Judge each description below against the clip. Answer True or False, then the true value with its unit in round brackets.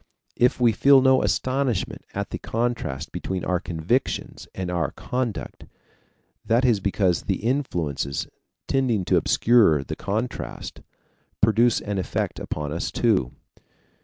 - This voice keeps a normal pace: False (130 wpm)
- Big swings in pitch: True (5.7 semitones)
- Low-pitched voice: True (105 Hz)